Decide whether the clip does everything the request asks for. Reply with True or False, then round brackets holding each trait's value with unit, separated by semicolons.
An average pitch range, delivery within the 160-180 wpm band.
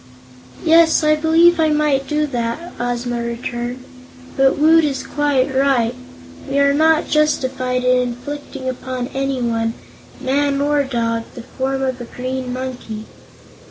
False (3.1 semitones; 135 wpm)